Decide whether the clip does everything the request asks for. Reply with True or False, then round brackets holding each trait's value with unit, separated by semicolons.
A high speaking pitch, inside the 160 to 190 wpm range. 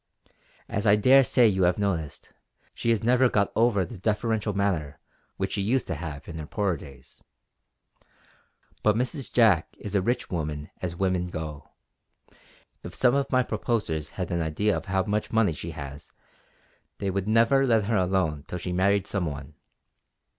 False (100 Hz; 175 wpm)